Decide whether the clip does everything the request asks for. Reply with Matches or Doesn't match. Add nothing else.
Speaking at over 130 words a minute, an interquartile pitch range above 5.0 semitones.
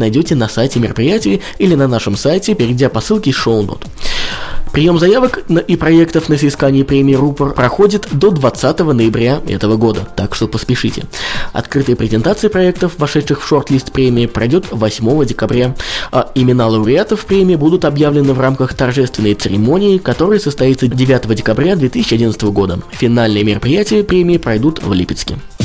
Matches